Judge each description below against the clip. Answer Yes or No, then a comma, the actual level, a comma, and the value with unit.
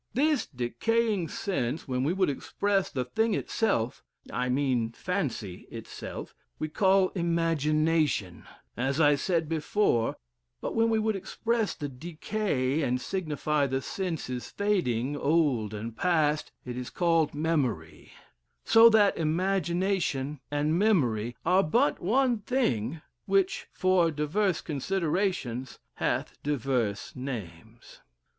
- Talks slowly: Yes, slow, 120 wpm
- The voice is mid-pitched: Yes, medium, 155 Hz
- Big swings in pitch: Yes, wide, 7.1 semitones